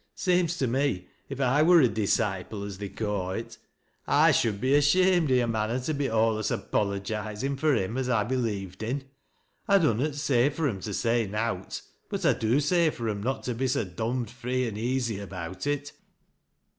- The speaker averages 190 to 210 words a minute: Yes, average, 195 wpm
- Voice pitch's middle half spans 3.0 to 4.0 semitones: No, average, 4.8 semitones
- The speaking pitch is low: Yes, low, 120 Hz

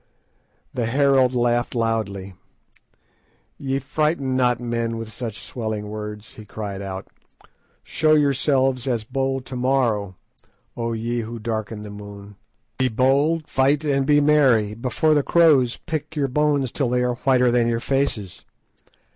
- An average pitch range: Yes, average, 3.7 semitones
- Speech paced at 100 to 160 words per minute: Yes, average, 145 wpm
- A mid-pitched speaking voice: No, low, 125 Hz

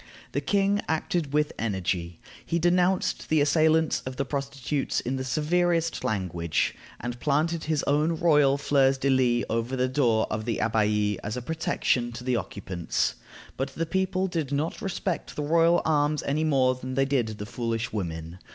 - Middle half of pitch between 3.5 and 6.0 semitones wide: Yes, wide, 5.5 semitones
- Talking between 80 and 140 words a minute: No, average, 170 wpm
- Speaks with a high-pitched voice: No, medium, 140 Hz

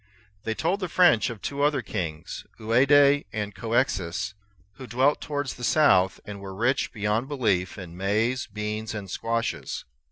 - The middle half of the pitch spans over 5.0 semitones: Yes, wide, 5.4 semitones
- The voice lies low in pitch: Yes, low, 115 Hz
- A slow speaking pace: No, average, 155 wpm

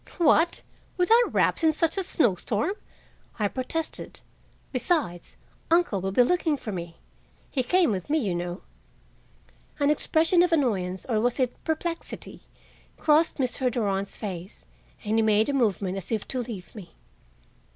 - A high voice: Yes, high, 245 Hz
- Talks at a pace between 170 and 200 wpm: No, average, 150 wpm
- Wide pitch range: Yes, wide, 8.2 semitones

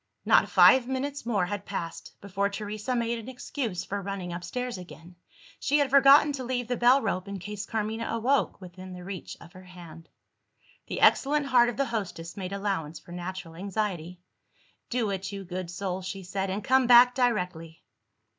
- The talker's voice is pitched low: No, high, 200 Hz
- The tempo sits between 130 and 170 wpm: No, average, 180 wpm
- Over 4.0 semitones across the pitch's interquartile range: Yes, average, 5.2 semitones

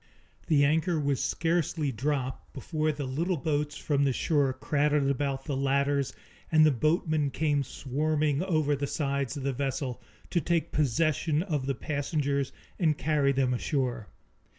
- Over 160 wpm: No, average, 150 wpm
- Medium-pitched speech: Yes, medium, 145 Hz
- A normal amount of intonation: No, narrow, 2.1 semitones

